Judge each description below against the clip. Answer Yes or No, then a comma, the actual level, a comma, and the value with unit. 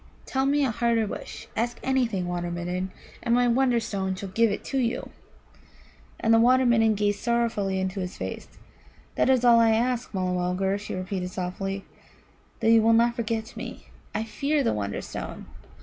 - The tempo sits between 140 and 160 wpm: No, average, 170 wpm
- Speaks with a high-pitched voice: Yes, high, 225 Hz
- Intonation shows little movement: No, average, 3.9 semitones